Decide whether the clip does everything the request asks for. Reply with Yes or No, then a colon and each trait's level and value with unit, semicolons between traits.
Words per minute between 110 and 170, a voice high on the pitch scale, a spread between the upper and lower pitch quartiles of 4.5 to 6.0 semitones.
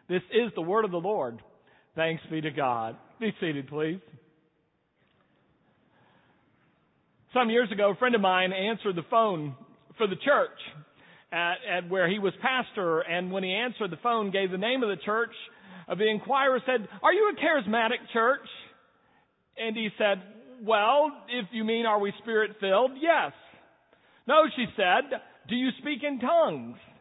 Yes: average, 160 wpm; high, 220 Hz; average, 5.2 semitones